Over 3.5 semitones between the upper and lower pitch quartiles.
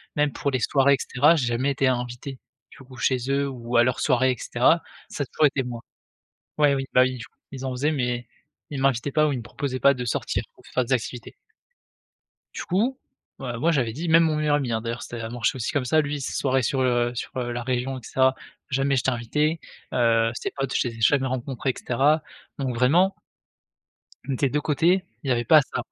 No: average, 2.8 semitones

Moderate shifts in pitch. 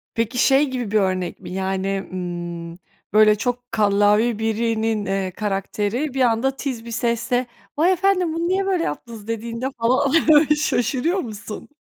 Yes: average, 4.3 semitones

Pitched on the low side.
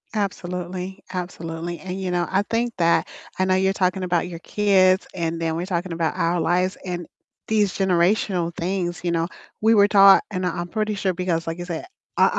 No: medium, 180 Hz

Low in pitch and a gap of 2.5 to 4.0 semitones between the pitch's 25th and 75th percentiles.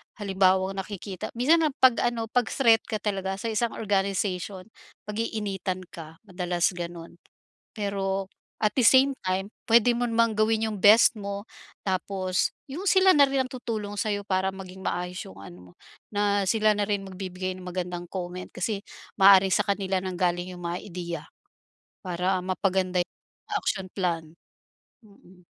No: high, 195 Hz; average, 2.9 semitones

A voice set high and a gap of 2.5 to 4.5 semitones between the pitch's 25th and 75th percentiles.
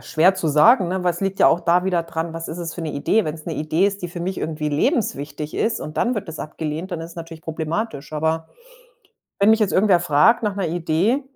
No: medium, 170 Hz; average, 3.5 semitones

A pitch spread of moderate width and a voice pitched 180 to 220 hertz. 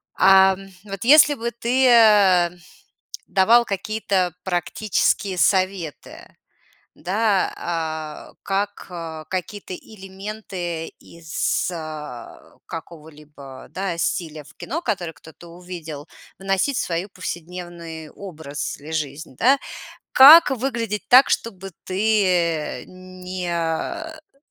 Yes: average, 4.2 semitones; medium, 185 Hz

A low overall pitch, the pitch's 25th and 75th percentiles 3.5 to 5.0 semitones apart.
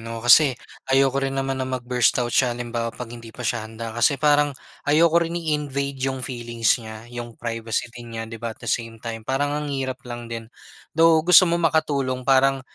No: low, 130 Hz; average, 3.1 semitones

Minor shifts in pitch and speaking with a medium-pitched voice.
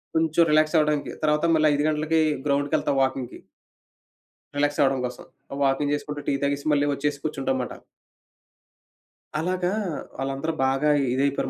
Yes: narrow, 1.8 semitones; medium, 145 Hz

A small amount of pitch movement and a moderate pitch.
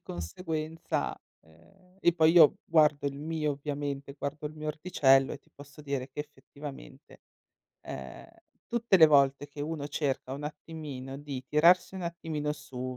Yes: narrow, 2.3 semitones; medium, 150 Hz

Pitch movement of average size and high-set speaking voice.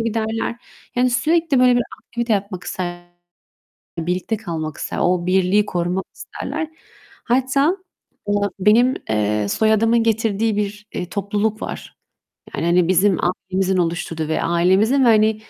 Yes: average, 4.2 semitones; high, 205 Hz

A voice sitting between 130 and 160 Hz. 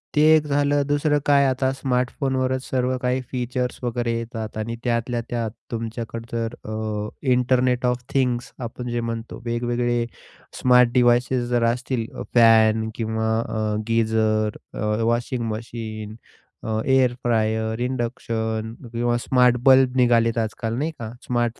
No: low, 120 Hz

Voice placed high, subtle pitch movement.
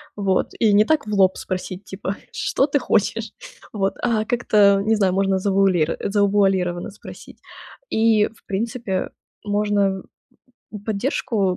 Yes: high, 200 Hz; narrow, 2.1 semitones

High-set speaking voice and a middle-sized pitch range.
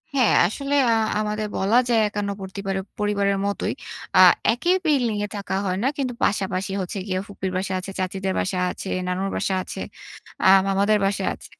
No: high, 200 Hz; narrow, 2.0 semitones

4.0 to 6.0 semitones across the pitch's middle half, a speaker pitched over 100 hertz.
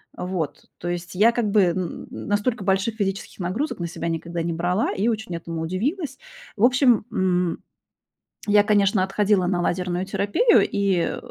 No: average, 3.3 semitones; high, 190 Hz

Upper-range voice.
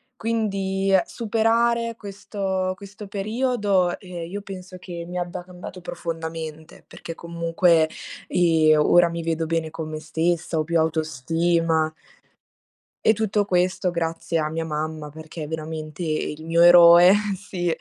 No: medium, 170 Hz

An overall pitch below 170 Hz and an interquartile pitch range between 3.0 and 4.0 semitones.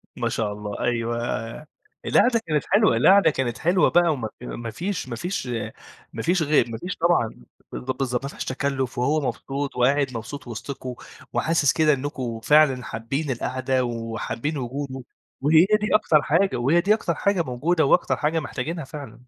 No: medium, 140 Hz; average, 5.0 semitones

